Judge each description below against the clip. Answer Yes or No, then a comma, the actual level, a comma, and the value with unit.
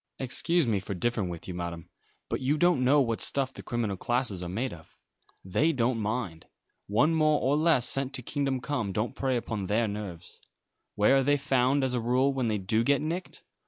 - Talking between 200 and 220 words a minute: Yes, fast, 205 wpm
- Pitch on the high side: No, low, 125 Hz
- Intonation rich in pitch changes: No, average, 4.8 semitones